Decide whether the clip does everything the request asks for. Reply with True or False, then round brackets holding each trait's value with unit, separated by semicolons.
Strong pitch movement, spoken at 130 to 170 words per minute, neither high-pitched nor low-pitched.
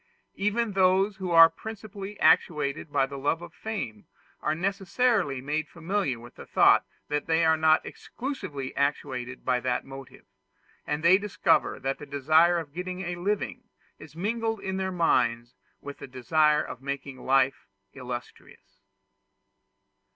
True (5.8 semitones; 145 wpm; 160 Hz)